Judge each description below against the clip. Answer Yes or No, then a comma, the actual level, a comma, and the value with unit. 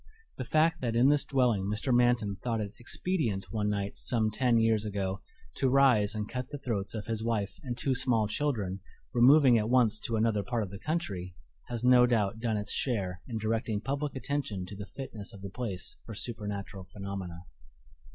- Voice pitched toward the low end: Yes, low, 110 Hz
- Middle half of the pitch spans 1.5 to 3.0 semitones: No, average, 3.6 semitones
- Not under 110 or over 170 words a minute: No, average, 190 wpm